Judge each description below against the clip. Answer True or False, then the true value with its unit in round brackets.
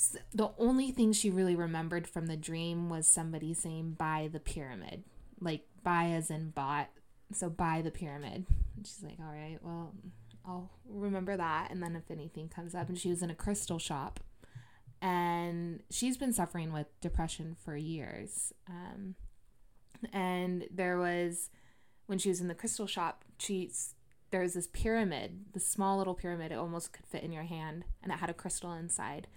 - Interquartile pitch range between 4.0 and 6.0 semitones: False (2.7 semitones)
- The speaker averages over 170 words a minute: True (180 wpm)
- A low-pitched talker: False (170 Hz)